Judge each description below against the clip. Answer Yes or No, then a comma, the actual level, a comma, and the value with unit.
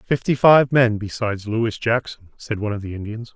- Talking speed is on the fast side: No, average, 195 wpm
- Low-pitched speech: Yes, low, 115 Hz